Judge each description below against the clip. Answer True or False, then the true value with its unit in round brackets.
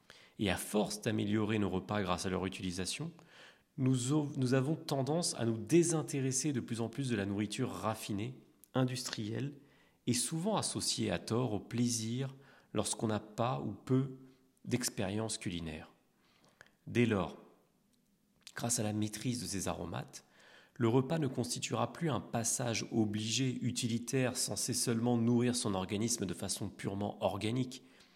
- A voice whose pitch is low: True (120 Hz)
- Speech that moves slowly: True (140 wpm)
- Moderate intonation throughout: True (3.8 semitones)